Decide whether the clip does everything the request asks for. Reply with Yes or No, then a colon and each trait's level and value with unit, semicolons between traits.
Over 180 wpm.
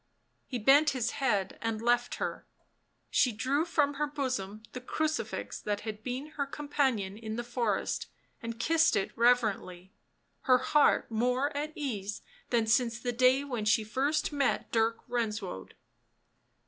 No: average, 150 wpm